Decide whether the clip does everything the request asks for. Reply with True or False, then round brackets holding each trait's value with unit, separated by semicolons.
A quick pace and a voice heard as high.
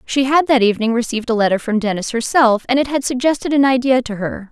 True (240 wpm; 245 Hz)